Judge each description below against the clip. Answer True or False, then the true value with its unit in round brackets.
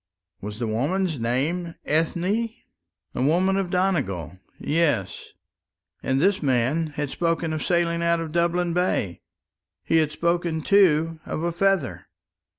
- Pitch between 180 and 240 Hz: False (165 Hz)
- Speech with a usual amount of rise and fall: True (3.8 semitones)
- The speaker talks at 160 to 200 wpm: False (135 wpm)